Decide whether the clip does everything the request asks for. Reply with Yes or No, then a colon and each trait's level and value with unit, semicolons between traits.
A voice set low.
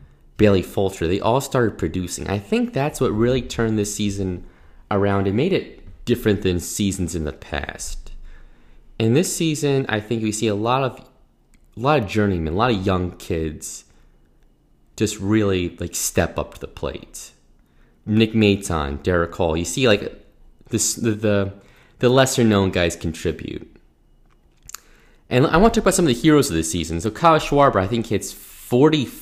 Yes: low, 100 Hz